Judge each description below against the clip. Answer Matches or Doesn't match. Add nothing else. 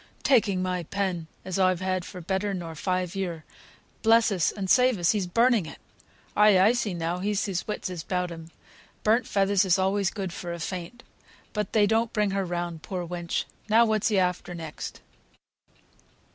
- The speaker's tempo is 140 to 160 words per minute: Doesn't match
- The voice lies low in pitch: Doesn't match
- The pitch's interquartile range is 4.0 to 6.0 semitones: Doesn't match